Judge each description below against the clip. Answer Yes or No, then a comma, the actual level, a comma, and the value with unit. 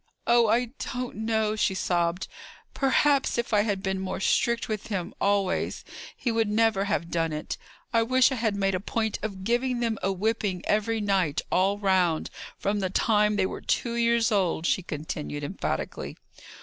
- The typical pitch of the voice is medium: No, high, 205 Hz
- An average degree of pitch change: Yes, average, 3.3 semitones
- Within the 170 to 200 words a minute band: Yes, average, 175 wpm